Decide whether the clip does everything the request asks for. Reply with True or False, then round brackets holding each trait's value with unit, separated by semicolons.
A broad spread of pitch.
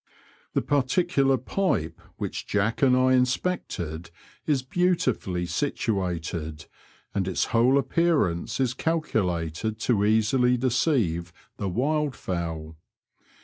True (7.6 semitones)